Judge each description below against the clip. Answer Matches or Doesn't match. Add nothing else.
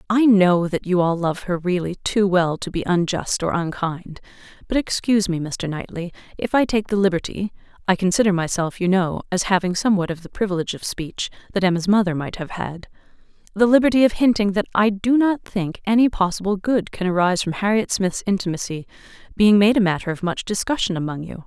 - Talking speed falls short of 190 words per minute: Doesn't match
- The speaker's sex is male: Doesn't match